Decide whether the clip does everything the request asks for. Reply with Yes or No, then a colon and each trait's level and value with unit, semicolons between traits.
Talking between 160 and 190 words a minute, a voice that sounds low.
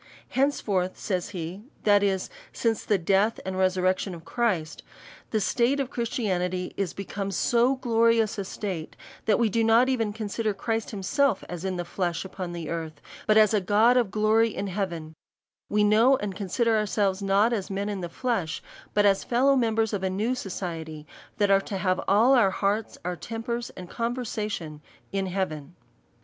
No: average, 180 wpm; high, 205 Hz